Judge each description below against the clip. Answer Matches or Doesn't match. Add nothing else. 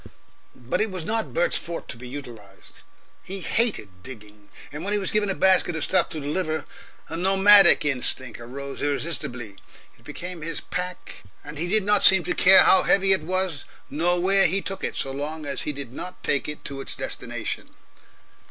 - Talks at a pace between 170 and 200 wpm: Matches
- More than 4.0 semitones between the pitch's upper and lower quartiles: Matches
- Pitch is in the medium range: Matches